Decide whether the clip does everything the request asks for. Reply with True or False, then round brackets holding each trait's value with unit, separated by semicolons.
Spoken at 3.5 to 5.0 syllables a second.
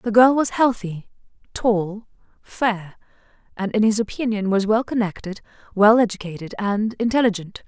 True (4.7 syllables/s)